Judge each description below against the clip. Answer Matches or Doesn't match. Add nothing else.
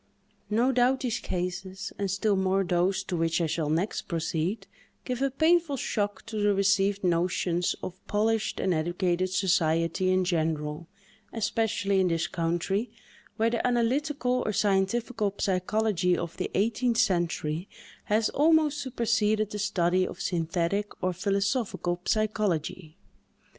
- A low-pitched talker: Doesn't match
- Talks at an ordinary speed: Doesn't match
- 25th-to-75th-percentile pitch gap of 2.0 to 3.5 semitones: Doesn't match